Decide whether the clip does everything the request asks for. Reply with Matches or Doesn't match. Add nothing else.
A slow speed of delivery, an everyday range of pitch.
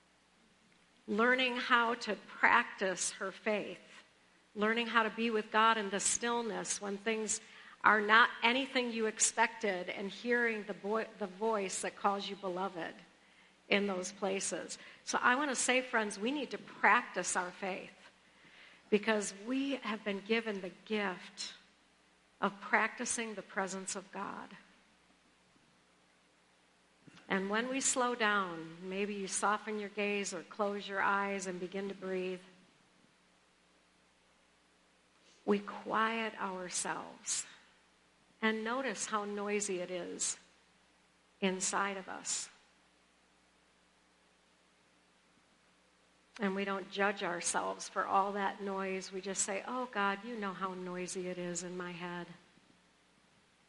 Matches